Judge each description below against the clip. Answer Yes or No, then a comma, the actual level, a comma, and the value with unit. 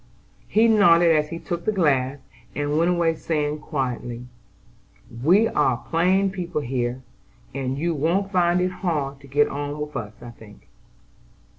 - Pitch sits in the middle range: Yes, medium, 150 Hz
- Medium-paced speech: Yes, average, 155 wpm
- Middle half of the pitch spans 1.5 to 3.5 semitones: No, average, 4.3 semitones